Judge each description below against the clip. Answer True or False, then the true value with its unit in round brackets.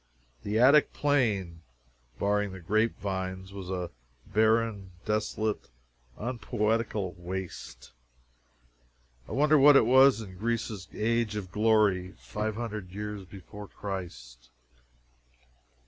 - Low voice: True (105 Hz)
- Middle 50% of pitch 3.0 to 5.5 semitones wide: True (3.3 semitones)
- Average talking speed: False (105 wpm)